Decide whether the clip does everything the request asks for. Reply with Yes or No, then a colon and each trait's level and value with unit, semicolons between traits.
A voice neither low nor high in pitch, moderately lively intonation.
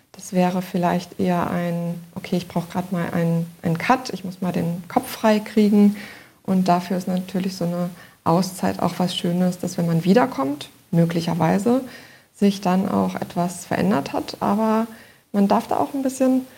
Yes: medium, 180 Hz; average, 3.0 semitones